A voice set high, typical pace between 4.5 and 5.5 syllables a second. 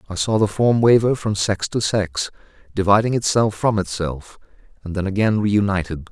No: low, 100 Hz; 5.0 syllables/s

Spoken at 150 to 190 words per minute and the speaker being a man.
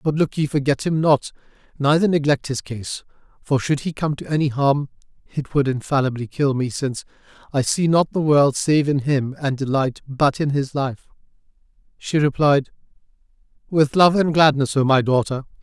Yes: average, 175 wpm; male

